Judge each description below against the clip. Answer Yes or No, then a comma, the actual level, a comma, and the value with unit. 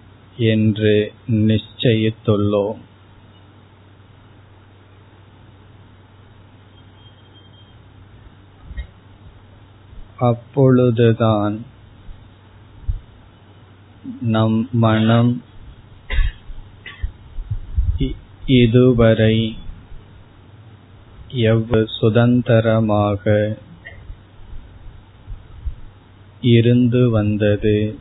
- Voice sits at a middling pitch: No, low, 105 Hz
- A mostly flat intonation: Yes, narrow, 1.7 semitones